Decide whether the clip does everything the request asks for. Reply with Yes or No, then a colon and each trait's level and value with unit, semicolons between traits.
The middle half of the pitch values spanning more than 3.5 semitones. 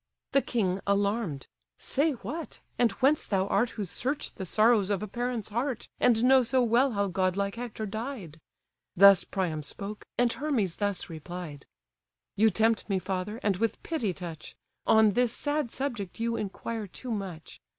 Yes: average, 4.2 semitones